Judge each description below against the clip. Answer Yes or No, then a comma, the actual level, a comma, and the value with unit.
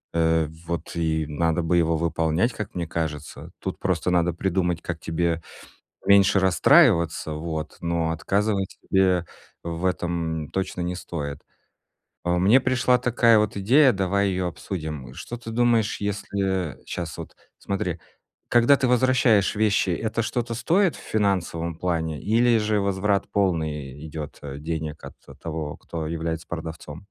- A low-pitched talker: Yes, very low, 90 Hz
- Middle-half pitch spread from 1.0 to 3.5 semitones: No, average, 4.2 semitones